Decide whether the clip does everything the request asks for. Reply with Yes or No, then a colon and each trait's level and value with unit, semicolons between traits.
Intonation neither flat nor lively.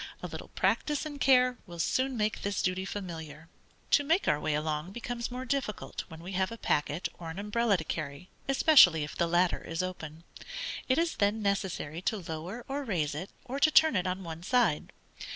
No: wide, 7.0 semitones